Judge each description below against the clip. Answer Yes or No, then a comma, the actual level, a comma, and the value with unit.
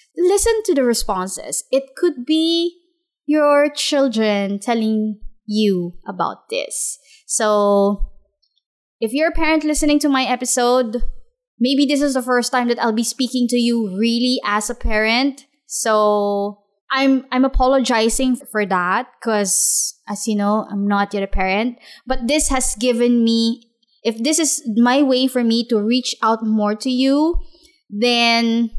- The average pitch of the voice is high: Yes, high, 245 Hz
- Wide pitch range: No, average, 4.4 semitones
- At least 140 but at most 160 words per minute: Yes, average, 150 wpm